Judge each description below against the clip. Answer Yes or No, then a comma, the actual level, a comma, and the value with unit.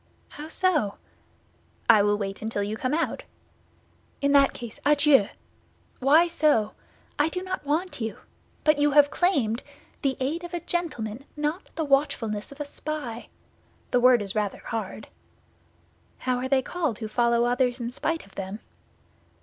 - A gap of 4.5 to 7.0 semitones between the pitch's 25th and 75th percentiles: Yes, average, 5.3 semitones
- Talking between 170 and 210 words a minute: No, average, 160 wpm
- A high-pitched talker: Yes, very high, 265 Hz